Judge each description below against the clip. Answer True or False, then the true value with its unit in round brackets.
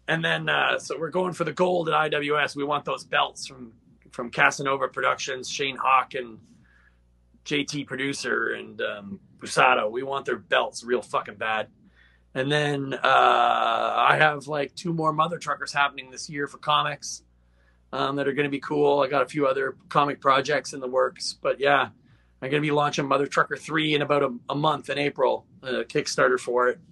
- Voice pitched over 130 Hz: True (140 Hz)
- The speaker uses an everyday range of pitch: True (3.1 semitones)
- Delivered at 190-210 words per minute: True (195 wpm)